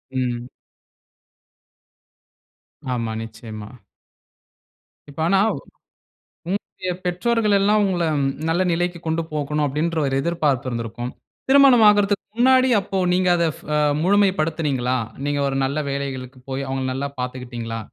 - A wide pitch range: Yes, wide, 6.4 semitones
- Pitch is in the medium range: Yes, medium, 150 Hz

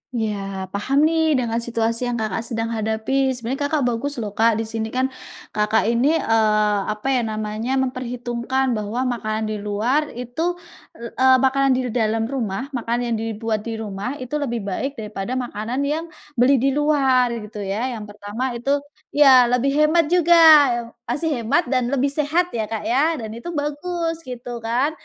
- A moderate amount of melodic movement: Yes, average, 3.8 semitones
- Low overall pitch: No, high, 245 Hz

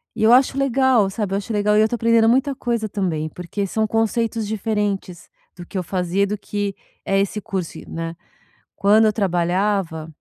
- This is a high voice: Yes, high, 205 Hz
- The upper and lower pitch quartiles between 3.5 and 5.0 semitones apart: No, average, 3.1 semitones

